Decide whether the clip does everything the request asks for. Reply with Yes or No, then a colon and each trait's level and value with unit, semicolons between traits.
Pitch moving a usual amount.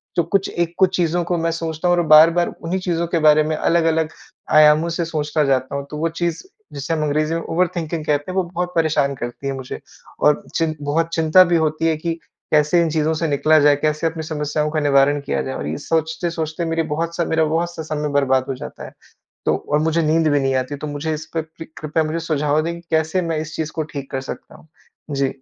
No: narrow, 1.9 semitones